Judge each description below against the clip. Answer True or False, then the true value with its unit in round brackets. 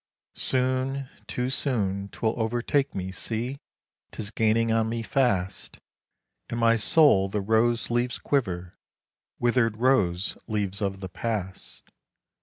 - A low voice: True (115 Hz)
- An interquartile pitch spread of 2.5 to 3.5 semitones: False (4.0 semitones)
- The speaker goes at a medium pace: False (120 wpm)